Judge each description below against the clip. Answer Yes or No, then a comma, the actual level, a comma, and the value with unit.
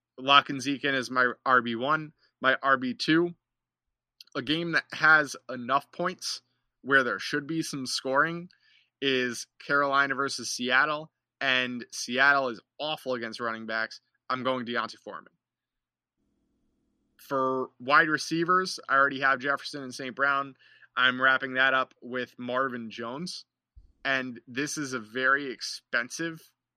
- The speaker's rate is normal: No, slow, 130 wpm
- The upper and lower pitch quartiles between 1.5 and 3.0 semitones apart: Yes, average, 2.7 semitones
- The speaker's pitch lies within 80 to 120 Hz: No, low, 135 Hz